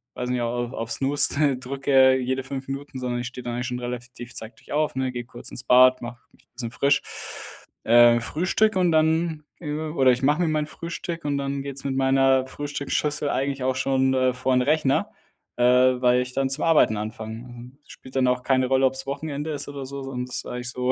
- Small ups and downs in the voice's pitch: Yes, narrow, 2.2 semitones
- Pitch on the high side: No, low, 130 Hz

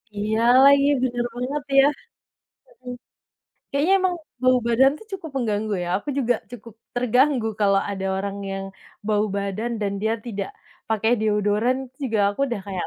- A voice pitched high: Yes, high, 225 Hz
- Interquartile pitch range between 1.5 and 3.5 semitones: No, average, 3.9 semitones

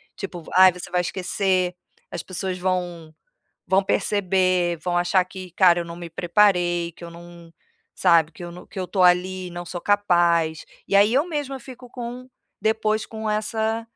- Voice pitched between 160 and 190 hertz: Yes, medium, 185 Hz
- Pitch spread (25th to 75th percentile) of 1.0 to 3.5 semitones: Yes, average, 2.9 semitones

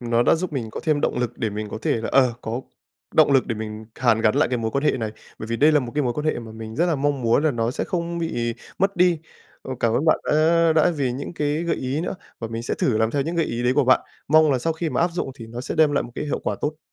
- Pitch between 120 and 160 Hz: Yes, low, 135 Hz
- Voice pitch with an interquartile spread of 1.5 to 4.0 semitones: No, average, 5.1 semitones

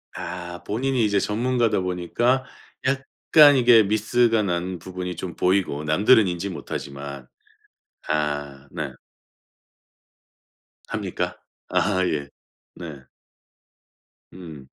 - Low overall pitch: Yes, very low, 90 Hz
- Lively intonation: Yes, wide, 6.5 semitones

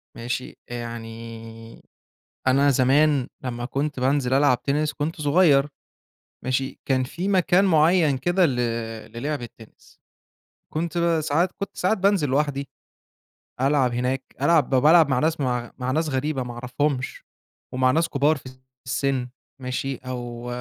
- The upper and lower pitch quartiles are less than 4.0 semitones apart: Yes, average, 3.3 semitones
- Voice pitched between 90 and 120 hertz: No, low, 135 Hz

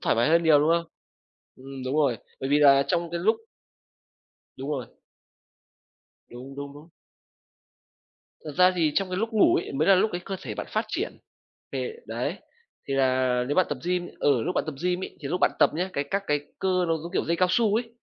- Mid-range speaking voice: Yes, medium, 165 Hz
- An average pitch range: Yes, average, 4.7 semitones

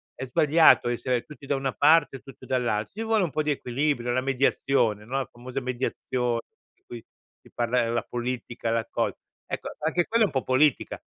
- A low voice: Yes, low, 130 Hz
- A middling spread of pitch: Yes, average, 3.1 semitones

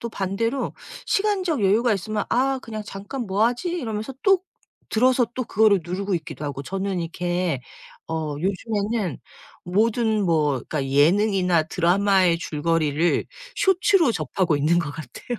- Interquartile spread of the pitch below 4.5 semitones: No, wide, 5.6 semitones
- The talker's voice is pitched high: Yes, high, 195 Hz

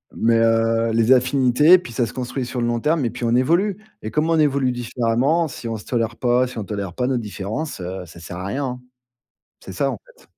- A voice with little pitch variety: No, average, 3.0 semitones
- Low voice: Yes, low, 120 Hz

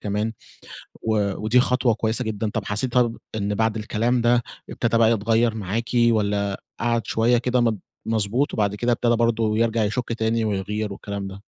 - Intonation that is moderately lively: No, narrow, 2.2 semitones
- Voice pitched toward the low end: Yes, low, 110 Hz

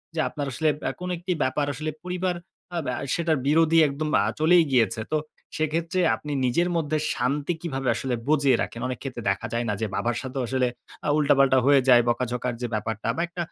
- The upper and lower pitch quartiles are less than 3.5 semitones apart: No, average, 4.5 semitones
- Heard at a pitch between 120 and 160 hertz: Yes, medium, 140 Hz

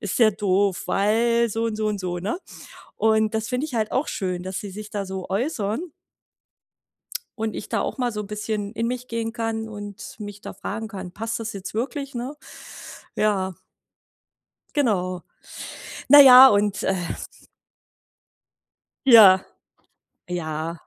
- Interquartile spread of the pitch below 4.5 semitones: Yes, average, 2.8 semitones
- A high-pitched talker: Yes, high, 215 Hz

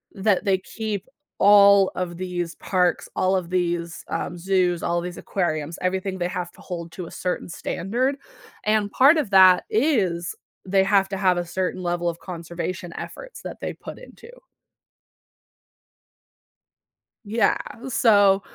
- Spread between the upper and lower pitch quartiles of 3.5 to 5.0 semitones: No, narrow, 2.5 semitones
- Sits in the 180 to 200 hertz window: Yes, medium, 185 Hz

